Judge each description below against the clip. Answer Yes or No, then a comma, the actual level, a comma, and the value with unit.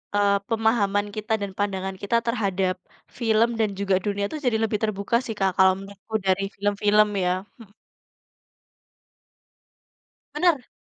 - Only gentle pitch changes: Yes, narrow, 2.1 semitones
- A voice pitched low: No, high, 205 Hz